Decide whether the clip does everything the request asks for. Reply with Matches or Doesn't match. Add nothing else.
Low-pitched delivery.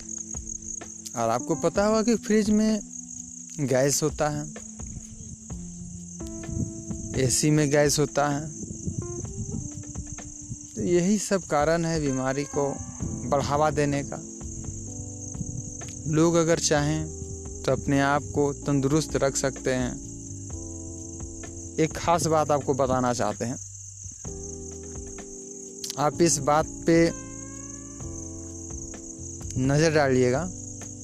Matches